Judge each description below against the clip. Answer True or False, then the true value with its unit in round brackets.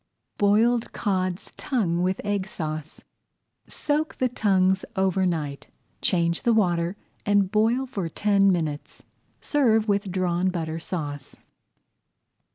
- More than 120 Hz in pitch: True (190 Hz)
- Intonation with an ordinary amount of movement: True (3.7 semitones)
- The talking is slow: True (115 wpm)